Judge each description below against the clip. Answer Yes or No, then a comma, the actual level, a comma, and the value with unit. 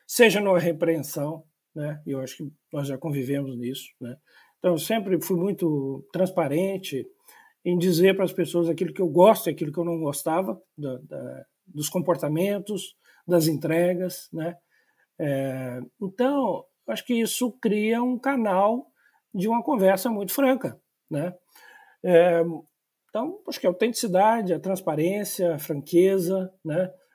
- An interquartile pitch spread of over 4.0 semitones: Yes, average, 4.5 semitones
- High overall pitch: No, medium, 180 Hz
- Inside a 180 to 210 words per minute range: No, average, 145 wpm